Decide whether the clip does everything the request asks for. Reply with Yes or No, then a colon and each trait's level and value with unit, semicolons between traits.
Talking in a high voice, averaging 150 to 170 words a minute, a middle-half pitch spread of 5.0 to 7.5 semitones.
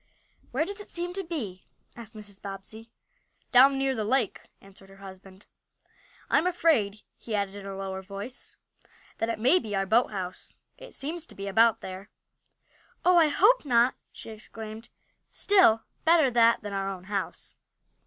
Yes: high, 220 Hz; average, 165 wpm; wide, 5.6 semitones